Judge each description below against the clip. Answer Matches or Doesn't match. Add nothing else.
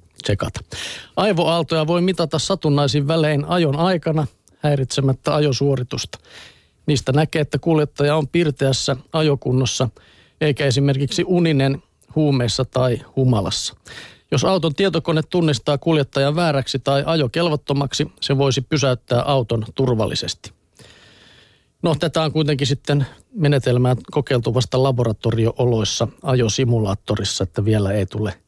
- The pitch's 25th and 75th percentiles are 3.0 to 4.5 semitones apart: Matches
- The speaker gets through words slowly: Doesn't match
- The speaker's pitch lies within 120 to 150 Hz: Matches